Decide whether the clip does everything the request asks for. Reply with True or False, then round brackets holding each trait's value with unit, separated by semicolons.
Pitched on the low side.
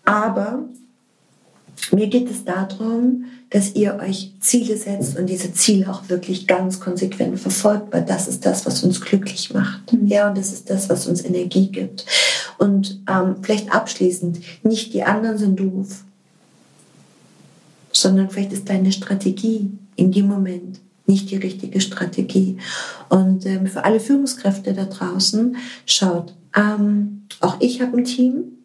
False (195 Hz)